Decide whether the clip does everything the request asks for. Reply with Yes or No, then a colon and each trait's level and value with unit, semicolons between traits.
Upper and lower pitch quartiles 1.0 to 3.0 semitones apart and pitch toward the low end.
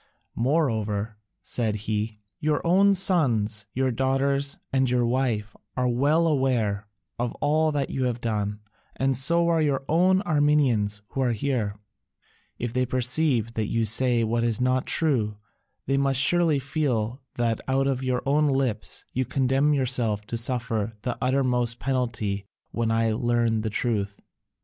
No: average, 3.5 semitones; low, 125 Hz